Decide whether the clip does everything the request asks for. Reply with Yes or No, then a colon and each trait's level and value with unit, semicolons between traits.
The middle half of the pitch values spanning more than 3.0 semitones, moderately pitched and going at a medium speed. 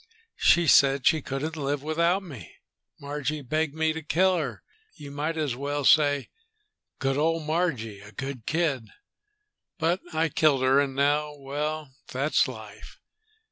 No: narrow, 2.6 semitones; medium, 145 Hz; average, 145 wpm